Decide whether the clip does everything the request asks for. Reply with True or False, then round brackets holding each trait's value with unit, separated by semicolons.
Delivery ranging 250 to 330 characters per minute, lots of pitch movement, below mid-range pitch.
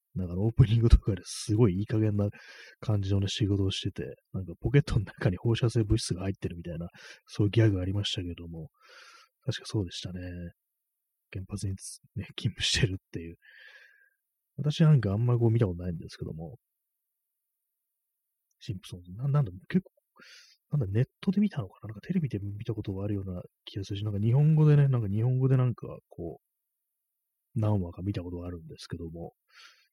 False (385 characters per minute; 5.7 semitones; 105 Hz)